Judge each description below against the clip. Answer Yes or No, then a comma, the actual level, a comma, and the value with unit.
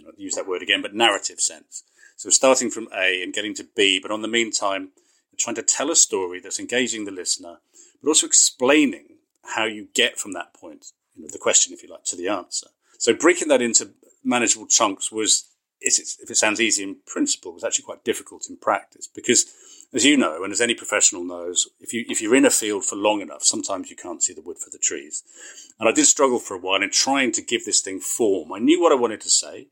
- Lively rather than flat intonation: Yes, wide, 5.8 semitones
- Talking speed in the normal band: No, fast, 240 wpm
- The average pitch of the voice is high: Yes, very high, 315 Hz